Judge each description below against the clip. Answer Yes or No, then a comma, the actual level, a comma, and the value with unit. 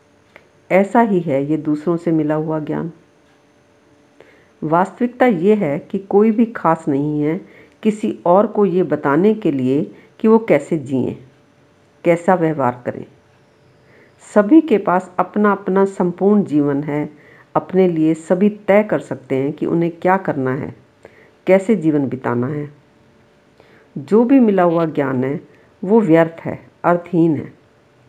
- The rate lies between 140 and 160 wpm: Yes, average, 145 wpm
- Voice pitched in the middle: Yes, medium, 170 Hz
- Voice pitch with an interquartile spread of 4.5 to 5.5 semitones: Yes, average, 5.0 semitones